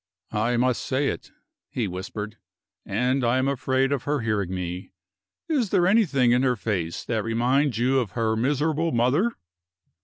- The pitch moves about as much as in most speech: Yes, average, 4.1 semitones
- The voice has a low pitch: Yes, low, 125 Hz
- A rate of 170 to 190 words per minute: No, average, 160 wpm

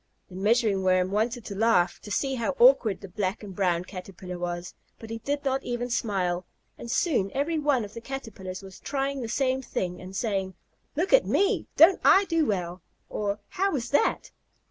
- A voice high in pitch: Yes, high, 220 Hz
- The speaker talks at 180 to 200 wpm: Yes, average, 190 wpm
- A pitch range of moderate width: No, wide, 6.2 semitones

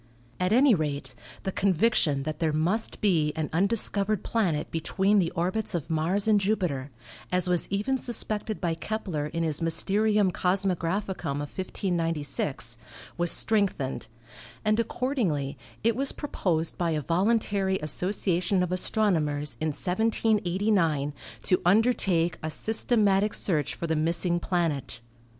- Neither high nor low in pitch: Yes, medium, 180 Hz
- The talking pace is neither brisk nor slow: No, slow, 130 wpm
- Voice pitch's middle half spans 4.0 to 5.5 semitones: Yes, average, 4.7 semitones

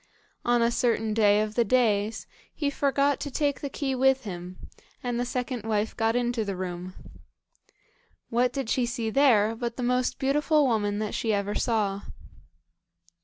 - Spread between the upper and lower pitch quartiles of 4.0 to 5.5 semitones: No, average, 3.4 semitones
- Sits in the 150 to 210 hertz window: No, high, 235 Hz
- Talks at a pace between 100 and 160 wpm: No, average, 170 wpm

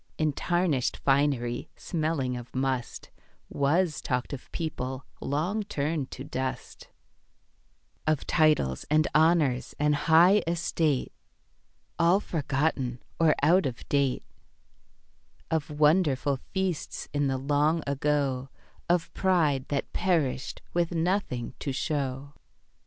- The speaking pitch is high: No, medium, 150 Hz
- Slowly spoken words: Yes, slow, 110 wpm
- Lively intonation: No, average, 3.6 semitones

